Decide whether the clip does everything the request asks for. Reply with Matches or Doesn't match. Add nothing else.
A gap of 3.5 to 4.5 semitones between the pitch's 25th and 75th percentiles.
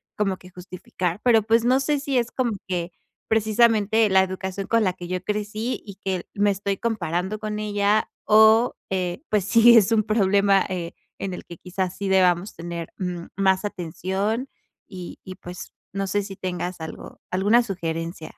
Doesn't match